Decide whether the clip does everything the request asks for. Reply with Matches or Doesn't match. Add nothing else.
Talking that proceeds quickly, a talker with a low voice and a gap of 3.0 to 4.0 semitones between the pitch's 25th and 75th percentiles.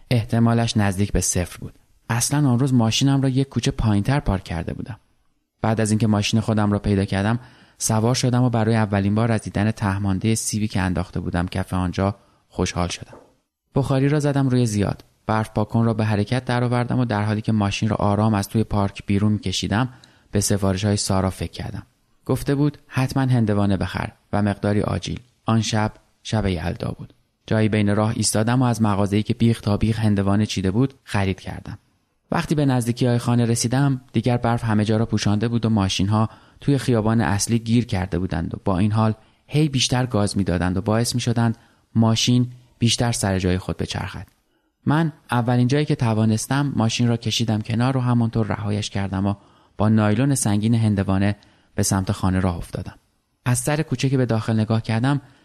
Matches